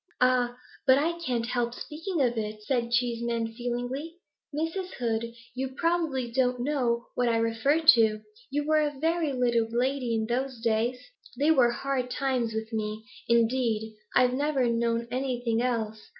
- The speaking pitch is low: No, high, 245 Hz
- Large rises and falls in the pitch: No, average, 2.8 semitones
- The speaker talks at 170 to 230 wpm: No, average, 155 wpm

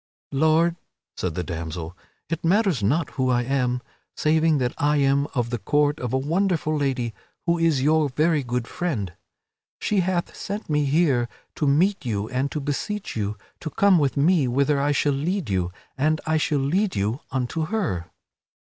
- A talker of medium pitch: Yes, medium, 145 Hz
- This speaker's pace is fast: No, average, 175 wpm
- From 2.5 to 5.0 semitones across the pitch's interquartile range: Yes, average, 4.7 semitones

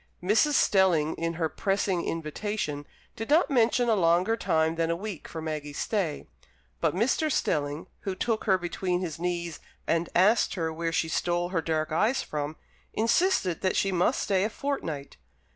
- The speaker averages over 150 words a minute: Yes, average, 170 wpm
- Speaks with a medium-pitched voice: Yes, medium, 175 Hz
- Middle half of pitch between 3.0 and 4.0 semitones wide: No, average, 4.6 semitones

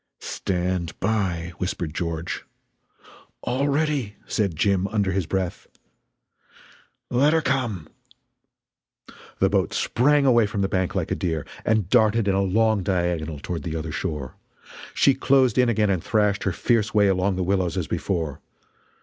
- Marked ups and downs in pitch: No, average, 4.2 semitones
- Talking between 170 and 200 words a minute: No, average, 150 wpm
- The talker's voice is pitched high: No, low, 100 Hz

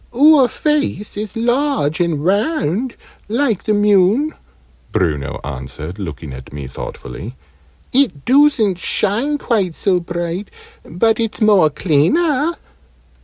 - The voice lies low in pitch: No, high, 205 Hz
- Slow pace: Yes, slow, 115 wpm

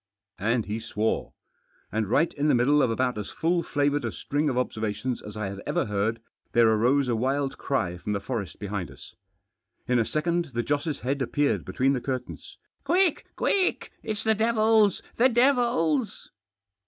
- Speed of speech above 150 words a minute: Yes, average, 180 wpm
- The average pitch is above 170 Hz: No, low, 130 Hz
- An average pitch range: No, wide, 6.8 semitones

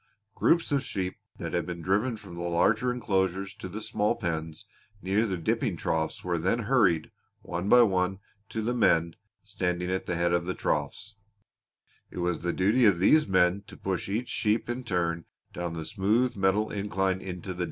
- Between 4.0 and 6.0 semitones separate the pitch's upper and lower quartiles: No, average, 3.6 semitones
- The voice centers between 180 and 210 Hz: No, very low, 95 Hz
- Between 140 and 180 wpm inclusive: No, average, 190 wpm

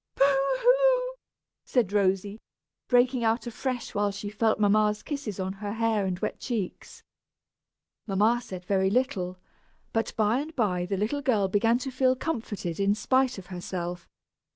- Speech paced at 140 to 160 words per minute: Yes, average, 155 wpm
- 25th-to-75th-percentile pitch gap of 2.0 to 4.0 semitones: No, average, 4.6 semitones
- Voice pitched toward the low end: No, high, 215 Hz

